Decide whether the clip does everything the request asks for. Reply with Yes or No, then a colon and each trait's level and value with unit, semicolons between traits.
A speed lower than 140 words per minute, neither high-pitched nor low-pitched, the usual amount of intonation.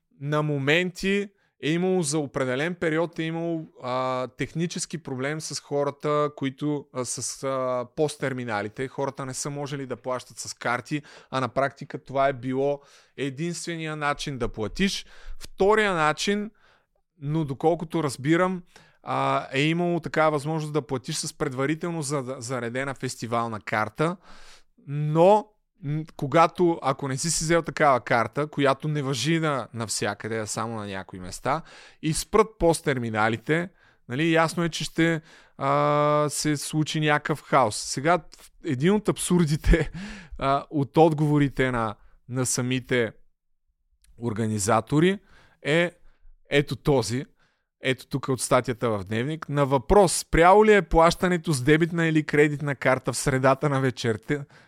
Yes: average, 130 wpm; medium, 145 Hz; average, 3.9 semitones